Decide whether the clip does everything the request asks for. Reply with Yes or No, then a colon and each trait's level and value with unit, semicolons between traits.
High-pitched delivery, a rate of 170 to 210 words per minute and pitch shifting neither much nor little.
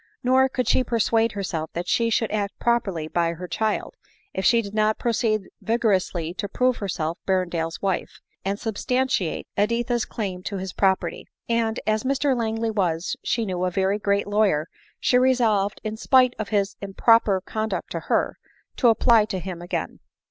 Yes: high, 210 Hz; average, 175 wpm; average, 3.6 semitones